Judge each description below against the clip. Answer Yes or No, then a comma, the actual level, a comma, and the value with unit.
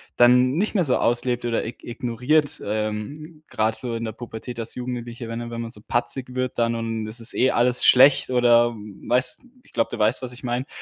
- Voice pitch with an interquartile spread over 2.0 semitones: No, narrow, 1.7 semitones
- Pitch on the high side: No, low, 120 Hz